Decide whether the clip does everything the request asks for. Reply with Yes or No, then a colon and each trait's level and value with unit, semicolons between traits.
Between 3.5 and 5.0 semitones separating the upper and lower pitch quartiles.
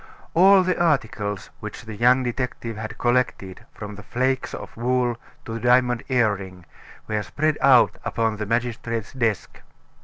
No: average, 3.0 semitones